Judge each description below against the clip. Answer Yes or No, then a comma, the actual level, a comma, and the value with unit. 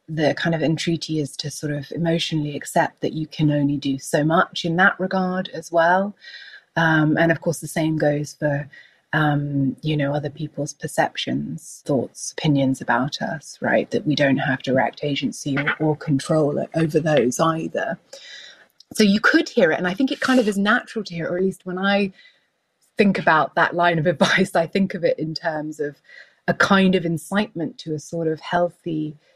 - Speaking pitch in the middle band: Yes, medium, 160 Hz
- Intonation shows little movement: No, average, 3.8 semitones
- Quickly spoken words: No, average, 195 wpm